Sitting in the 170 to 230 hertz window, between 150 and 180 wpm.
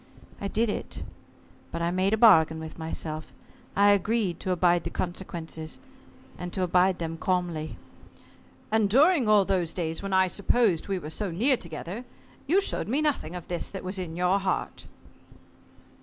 Yes: medium, 185 Hz; average, 170 wpm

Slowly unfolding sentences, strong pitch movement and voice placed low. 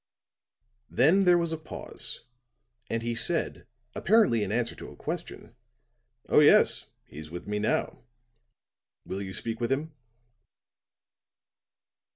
Yes: slow, 125 wpm; wide, 7.7 semitones; low, 120 Hz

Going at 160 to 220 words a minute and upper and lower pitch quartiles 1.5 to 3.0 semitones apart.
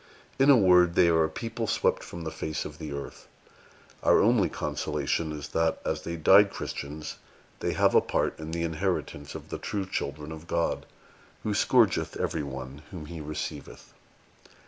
No: average, 175 wpm; average, 3.7 semitones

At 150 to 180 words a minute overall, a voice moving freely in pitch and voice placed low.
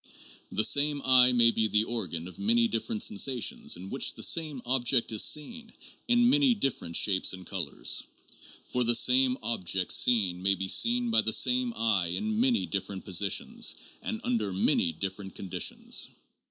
Yes: average, 165 wpm; wide, 6.5 semitones; low, 115 Hz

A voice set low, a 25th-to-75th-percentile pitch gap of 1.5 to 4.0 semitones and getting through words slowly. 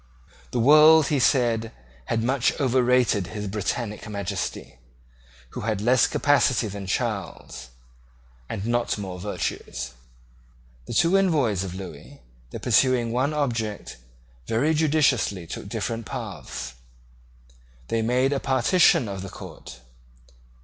No: low, 115 Hz; average, 4.9 semitones; slow, 120 wpm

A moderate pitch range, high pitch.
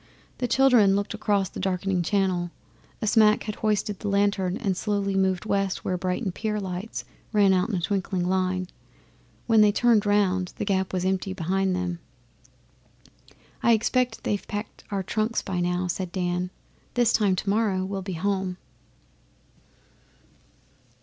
No: narrow, 2.3 semitones; high, 195 Hz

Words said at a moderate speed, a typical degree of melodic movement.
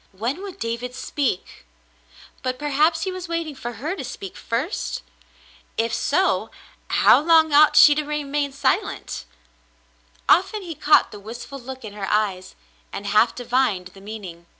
No: average, 150 wpm; wide, 5.8 semitones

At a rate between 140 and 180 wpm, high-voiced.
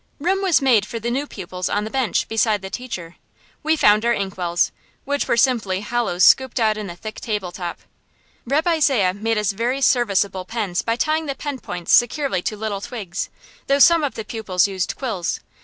No: average, 195 wpm; high, 220 Hz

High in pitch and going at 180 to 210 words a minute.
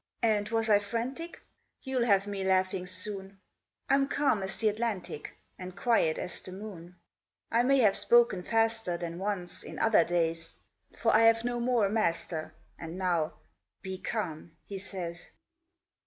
No: high, 200 Hz; average, 155 wpm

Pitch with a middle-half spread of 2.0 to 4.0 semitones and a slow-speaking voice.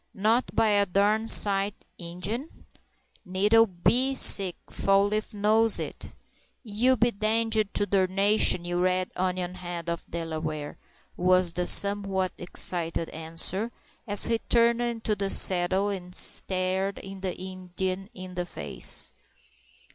Yes: average, 2.9 semitones; slow, 125 wpm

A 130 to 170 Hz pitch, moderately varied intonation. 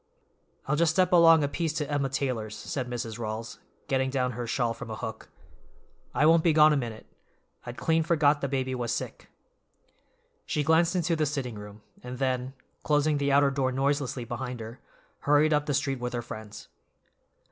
Yes: low, 135 Hz; average, 3.5 semitones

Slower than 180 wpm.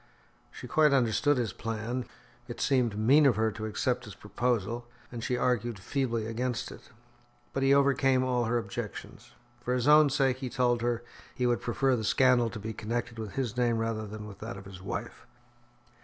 No: average, 190 wpm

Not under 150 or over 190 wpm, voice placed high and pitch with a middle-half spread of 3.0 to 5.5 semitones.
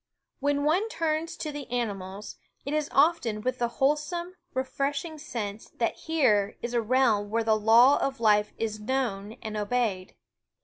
Yes: average, 175 wpm; high, 245 Hz; average, 5.2 semitones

